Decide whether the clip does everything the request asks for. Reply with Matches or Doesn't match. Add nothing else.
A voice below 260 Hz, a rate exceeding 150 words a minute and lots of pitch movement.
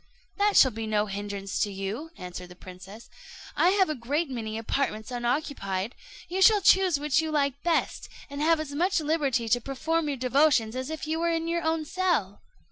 Doesn't match